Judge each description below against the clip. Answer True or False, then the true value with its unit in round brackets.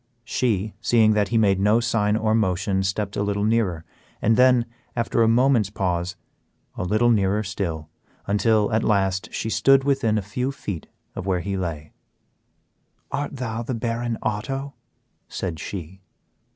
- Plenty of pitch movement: False (3.2 semitones)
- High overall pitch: False (105 Hz)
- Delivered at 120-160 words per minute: True (155 wpm)